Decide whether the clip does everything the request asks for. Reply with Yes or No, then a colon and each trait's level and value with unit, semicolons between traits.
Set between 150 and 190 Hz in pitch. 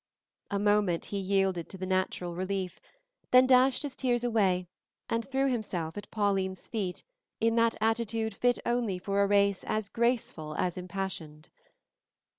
No: high, 200 Hz